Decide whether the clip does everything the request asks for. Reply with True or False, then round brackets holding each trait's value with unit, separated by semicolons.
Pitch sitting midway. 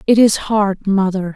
False (200 Hz)